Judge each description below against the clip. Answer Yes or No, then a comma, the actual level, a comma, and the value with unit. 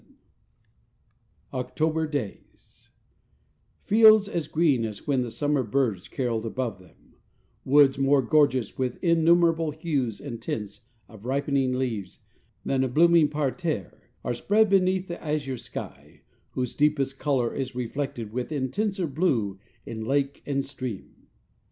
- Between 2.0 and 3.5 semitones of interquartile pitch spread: No, average, 4.3 semitones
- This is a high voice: No, low, 135 Hz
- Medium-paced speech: No, slow, 130 wpm